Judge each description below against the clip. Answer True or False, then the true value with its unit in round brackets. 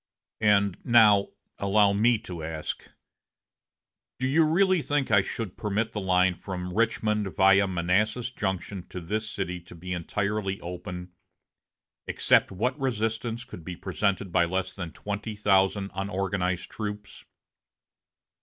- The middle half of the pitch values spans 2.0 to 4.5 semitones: True (2.9 semitones)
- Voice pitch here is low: True (100 Hz)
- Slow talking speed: True (130 wpm)